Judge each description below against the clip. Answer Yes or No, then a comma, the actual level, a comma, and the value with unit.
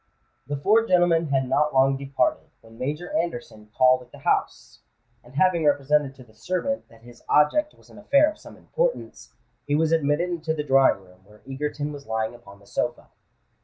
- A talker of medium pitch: Yes, medium, 145 Hz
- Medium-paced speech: Yes, average, 190 wpm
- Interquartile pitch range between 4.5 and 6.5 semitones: Yes, average, 5.1 semitones